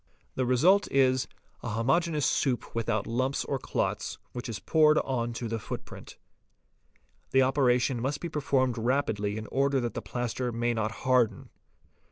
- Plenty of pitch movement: No, average, 2.9 semitones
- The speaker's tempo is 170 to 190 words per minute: No, average, 155 wpm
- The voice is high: No, low, 125 Hz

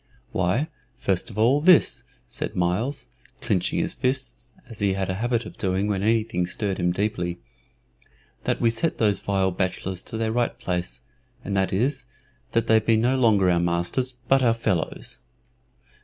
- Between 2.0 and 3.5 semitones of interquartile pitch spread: No, average, 4.3 semitones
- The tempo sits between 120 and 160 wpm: No, average, 170 wpm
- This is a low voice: Yes, low, 105 Hz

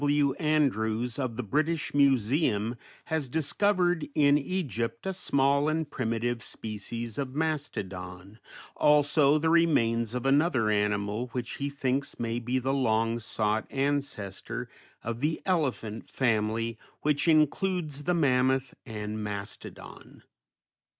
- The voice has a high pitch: No, low, 130 Hz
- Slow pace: Yes, slow, 120 wpm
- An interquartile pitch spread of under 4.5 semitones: No, average, 4.8 semitones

